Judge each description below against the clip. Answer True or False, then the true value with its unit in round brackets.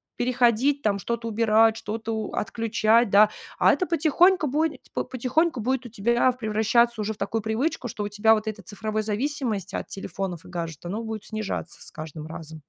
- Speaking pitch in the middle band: False (220 Hz)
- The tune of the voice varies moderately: True (3.1 semitones)